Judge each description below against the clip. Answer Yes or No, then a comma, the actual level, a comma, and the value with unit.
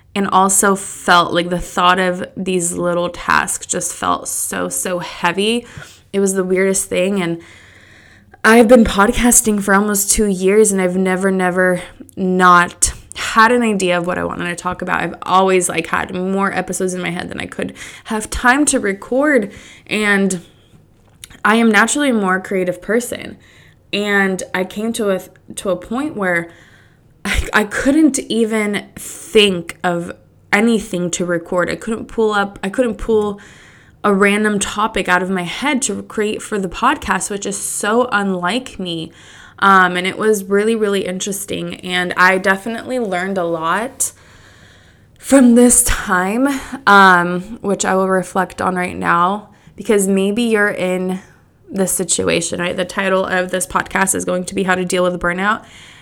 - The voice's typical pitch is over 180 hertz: Yes, high, 190 Hz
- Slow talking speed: No, average, 165 wpm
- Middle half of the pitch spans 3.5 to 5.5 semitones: No, average, 2.9 semitones